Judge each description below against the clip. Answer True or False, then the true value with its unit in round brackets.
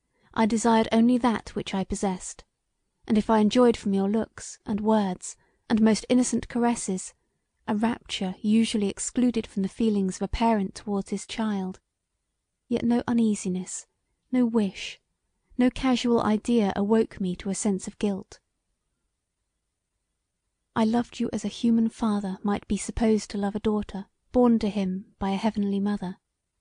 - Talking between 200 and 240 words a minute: False (155 wpm)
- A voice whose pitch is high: True (220 Hz)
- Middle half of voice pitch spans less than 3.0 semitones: True (2.5 semitones)